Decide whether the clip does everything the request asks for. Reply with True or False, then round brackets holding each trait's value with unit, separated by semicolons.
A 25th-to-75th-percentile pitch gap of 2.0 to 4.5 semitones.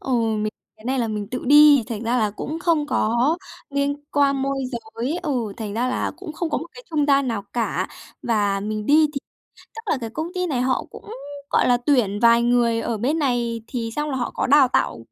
True (4.1 semitones)